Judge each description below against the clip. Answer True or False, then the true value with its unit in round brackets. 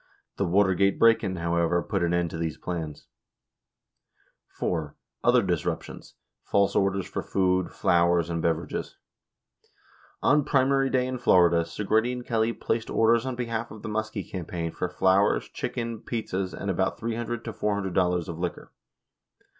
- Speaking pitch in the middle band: False (95 Hz)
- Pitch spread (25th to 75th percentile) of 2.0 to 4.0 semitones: False (4.8 semitones)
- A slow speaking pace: False (150 wpm)